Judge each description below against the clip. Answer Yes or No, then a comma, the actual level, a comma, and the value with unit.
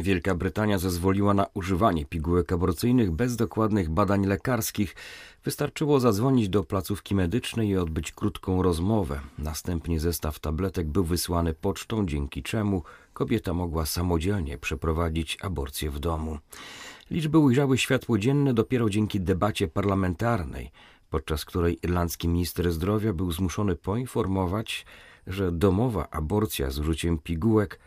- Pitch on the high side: No, very low, 95 Hz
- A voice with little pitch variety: No, average, 4.3 semitones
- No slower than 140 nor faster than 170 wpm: No, average, 125 wpm